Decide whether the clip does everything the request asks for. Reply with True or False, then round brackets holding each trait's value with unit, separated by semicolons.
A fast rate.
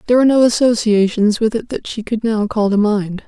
True (240 wpm)